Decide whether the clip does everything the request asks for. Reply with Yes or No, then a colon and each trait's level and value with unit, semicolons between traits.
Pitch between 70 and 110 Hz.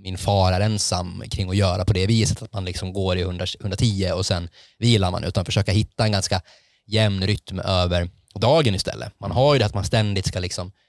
Yes: low, 100 Hz